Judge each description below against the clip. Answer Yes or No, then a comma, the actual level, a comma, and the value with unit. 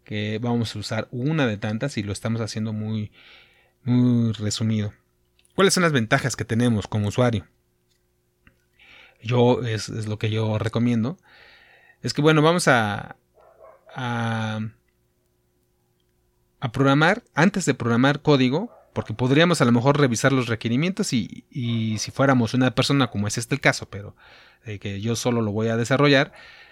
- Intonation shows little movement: No, average, 4.2 semitones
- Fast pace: No, average, 155 wpm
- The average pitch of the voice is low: Yes, low, 115 Hz